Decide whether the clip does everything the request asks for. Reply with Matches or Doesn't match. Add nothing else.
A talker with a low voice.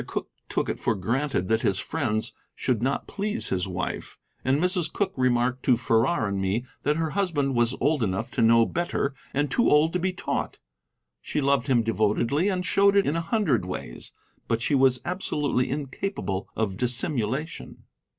Matches